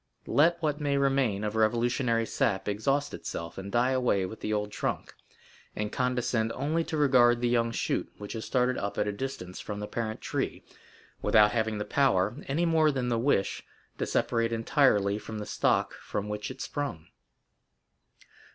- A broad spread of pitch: No, average, 4.4 semitones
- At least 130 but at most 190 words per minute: Yes, average, 175 wpm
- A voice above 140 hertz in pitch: No, low, 115 Hz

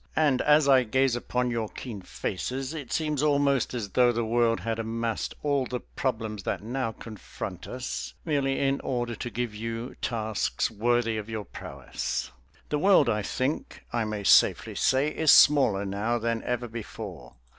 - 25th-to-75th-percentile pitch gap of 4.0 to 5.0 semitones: No, average, 3.4 semitones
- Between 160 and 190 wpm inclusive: Yes, average, 165 wpm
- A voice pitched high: No, low, 120 Hz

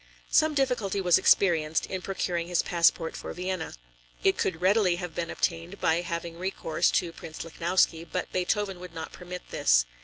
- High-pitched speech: No, medium, 175 Hz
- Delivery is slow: No, average, 165 wpm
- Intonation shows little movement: Yes, narrow, 2.0 semitones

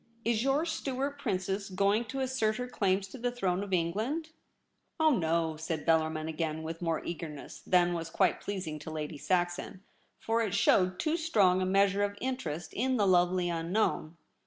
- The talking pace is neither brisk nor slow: Yes, average, 185 wpm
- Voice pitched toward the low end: No, high, 190 Hz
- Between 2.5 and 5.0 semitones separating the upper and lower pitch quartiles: No, wide, 5.6 semitones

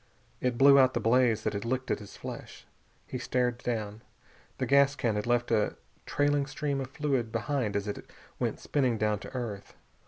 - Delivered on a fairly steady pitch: No, average, 3.7 semitones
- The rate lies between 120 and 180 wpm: No, average, 195 wpm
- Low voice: Yes, low, 120 Hz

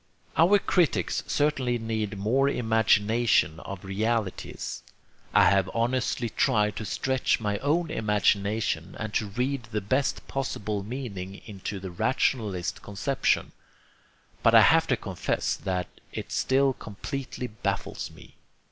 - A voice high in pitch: No, low, 110 Hz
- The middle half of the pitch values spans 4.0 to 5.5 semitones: Yes, average, 4.5 semitones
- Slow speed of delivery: Yes, slow, 125 wpm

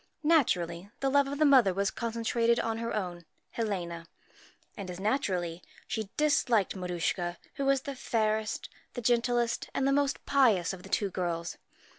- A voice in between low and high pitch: No, high, 220 Hz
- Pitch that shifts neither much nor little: No, wide, 6.3 semitones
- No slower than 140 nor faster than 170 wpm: Yes, average, 160 wpm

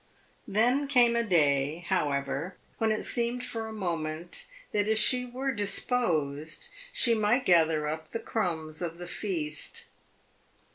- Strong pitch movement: Yes, wide, 6.7 semitones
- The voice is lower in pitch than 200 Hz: Yes, medium, 185 Hz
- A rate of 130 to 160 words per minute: Yes, average, 140 wpm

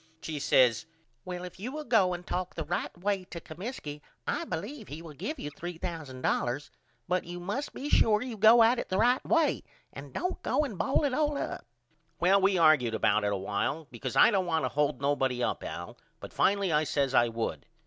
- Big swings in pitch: Yes, wide, 6.9 semitones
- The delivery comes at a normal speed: No, fast, 210 wpm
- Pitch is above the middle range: No, medium, 175 Hz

